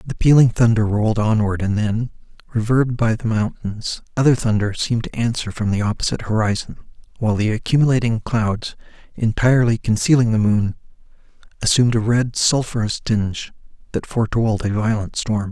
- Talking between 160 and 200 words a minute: No, average, 145 wpm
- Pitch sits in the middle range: No, low, 110 Hz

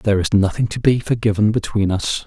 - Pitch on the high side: No, low, 105 Hz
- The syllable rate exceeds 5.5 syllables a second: Yes, 6.0 syllables/s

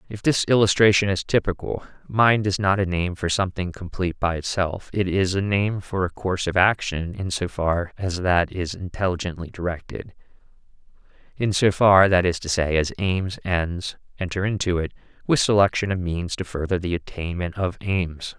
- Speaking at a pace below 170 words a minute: No, average, 180 wpm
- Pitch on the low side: Yes, very low, 90 Hz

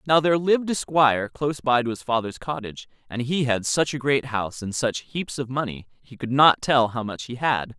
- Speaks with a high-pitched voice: No, low, 130 Hz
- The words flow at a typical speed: No, fast, 240 wpm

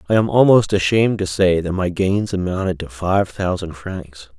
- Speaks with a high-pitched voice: No, very low, 95 Hz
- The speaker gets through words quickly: No, average, 190 wpm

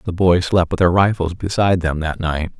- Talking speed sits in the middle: No, fast, 230 wpm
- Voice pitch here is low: Yes, very low, 90 Hz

